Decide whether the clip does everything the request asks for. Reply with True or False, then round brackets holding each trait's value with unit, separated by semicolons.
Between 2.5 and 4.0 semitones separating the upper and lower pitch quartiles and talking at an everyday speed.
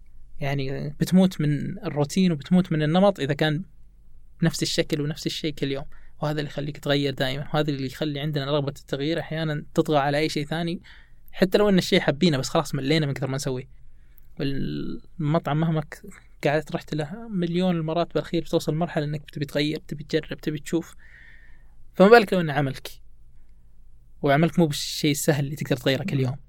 False (2.9 semitones; 170 wpm)